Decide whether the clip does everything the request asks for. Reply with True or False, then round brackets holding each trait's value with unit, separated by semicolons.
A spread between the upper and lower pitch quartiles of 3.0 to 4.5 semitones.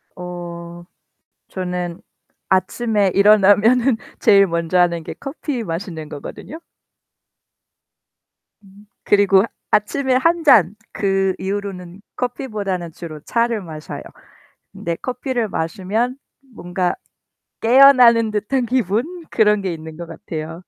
False (5.2 semitones)